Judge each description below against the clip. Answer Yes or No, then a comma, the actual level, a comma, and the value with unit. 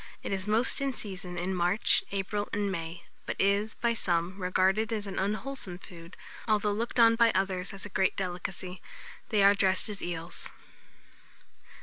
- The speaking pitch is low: No, high, 195 Hz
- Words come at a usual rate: Yes, average, 165 wpm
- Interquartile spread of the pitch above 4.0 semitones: No, average, 2.7 semitones